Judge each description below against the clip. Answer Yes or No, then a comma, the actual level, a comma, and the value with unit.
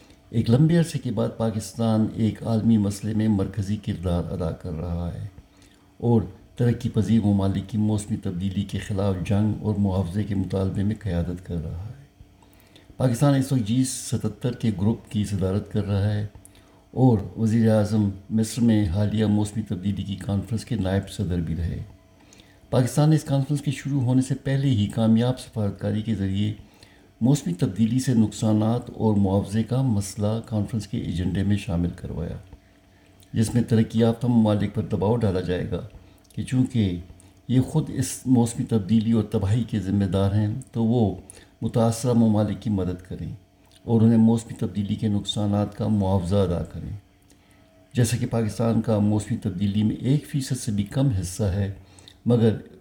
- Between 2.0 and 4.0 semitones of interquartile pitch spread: Yes, average, 2.9 semitones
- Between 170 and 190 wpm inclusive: No, average, 160 wpm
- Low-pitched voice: Yes, low, 105 Hz